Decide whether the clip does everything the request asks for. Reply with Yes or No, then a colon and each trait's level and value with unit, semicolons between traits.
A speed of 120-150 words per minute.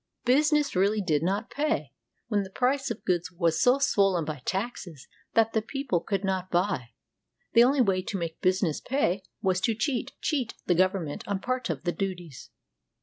No: average, 185 wpm